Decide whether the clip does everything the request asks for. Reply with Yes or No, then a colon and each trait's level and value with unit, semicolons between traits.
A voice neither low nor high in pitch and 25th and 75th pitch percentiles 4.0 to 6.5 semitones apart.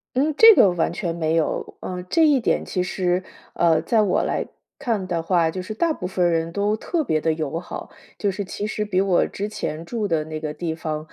Yes: medium, 180 Hz; average, 4.3 semitones